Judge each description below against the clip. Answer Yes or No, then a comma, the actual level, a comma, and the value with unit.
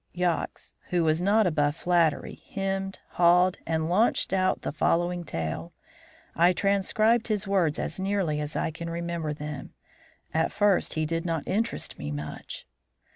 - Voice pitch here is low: No, medium, 170 Hz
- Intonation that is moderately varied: Yes, average, 3.5 semitones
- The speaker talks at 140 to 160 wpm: Yes, average, 155 wpm